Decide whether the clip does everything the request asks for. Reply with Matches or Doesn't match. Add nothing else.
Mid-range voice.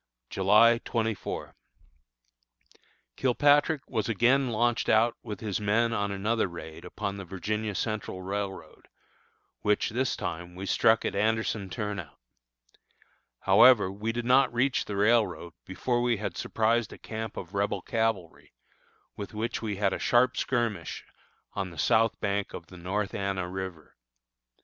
Doesn't match